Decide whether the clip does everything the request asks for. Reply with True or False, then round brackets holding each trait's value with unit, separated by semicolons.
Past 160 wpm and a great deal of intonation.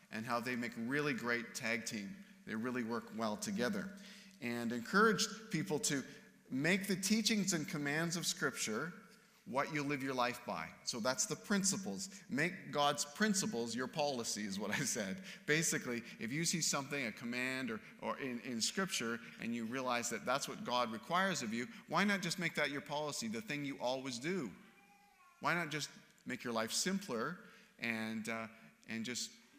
True (180 wpm; 8.4 semitones)